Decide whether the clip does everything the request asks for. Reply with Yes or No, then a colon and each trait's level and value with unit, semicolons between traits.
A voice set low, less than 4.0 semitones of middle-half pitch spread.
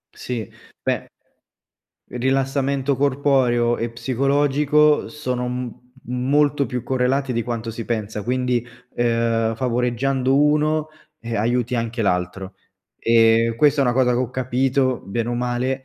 Yes: low, 125 Hz; narrow, 2.6 semitones